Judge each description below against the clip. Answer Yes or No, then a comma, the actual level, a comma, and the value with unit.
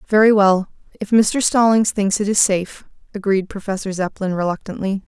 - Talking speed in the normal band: Yes, average, 150 wpm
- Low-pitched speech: No, high, 200 Hz